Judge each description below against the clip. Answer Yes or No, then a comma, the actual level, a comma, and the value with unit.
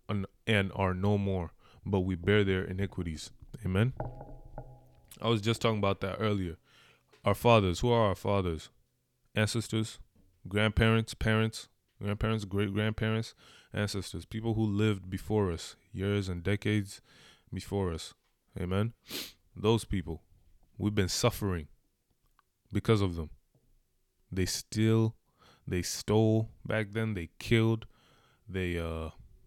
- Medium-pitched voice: No, low, 105 Hz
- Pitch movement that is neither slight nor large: Yes, average, 3.1 semitones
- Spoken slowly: Yes, slow, 120 wpm